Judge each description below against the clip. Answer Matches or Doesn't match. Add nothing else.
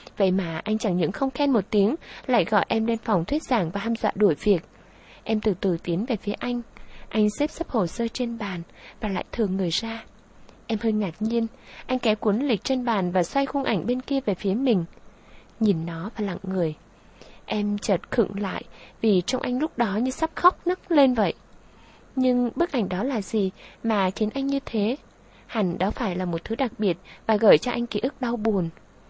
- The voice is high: Matches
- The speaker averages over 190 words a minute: Matches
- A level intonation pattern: Doesn't match